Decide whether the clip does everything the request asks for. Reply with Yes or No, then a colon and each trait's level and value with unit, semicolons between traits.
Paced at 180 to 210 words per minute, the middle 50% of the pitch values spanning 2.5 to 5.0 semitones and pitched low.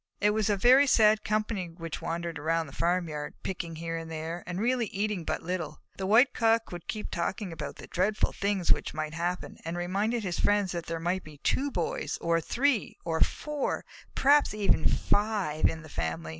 No: average, 195 wpm; average, 4.5 semitones; medium, 180 Hz